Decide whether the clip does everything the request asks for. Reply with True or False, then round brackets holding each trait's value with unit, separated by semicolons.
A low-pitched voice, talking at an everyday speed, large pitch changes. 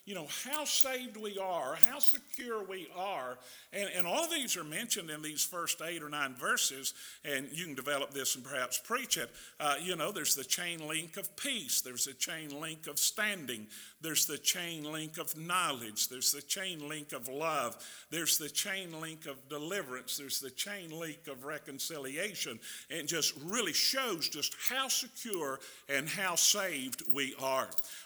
False (160 Hz; 180 wpm; 5.8 semitones)